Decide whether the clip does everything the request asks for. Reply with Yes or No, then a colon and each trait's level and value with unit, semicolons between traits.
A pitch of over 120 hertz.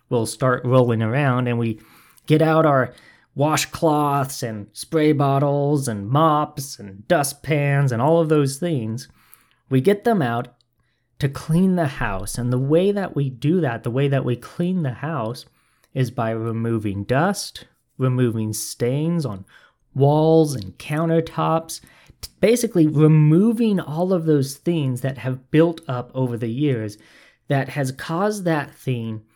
Yes: medium, 140 Hz